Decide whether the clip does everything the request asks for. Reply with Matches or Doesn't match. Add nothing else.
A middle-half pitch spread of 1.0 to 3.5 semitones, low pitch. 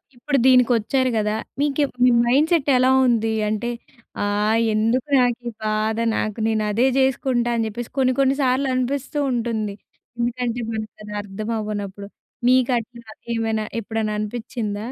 Doesn't match